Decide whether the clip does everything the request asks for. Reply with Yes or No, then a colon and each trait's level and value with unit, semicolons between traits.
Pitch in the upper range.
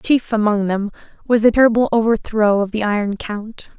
Yes: high, 215 Hz